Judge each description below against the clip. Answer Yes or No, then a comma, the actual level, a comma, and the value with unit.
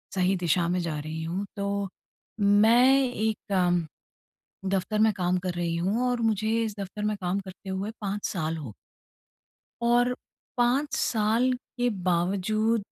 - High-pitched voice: Yes, high, 200 Hz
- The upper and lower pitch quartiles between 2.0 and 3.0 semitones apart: No, average, 3.5 semitones